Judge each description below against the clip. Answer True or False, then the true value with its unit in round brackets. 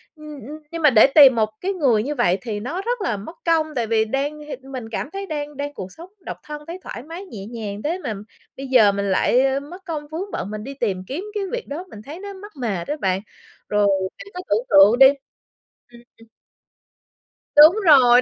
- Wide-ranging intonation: True (6.5 semitones)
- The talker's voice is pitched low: False (270 Hz)